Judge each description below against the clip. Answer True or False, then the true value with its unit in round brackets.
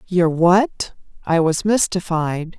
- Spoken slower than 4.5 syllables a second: True (3.3 syllables/s)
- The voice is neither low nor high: True (175 Hz)